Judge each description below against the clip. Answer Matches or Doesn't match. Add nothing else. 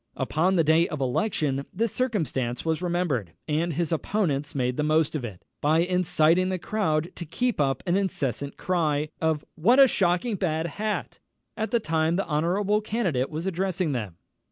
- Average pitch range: Matches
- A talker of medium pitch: Matches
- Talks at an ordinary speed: Matches